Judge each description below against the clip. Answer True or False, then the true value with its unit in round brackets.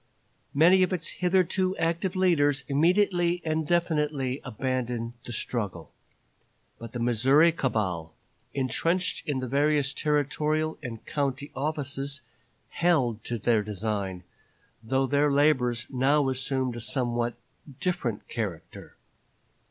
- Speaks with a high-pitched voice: False (140 Hz)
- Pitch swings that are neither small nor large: True (4.7 semitones)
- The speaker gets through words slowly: True (115 wpm)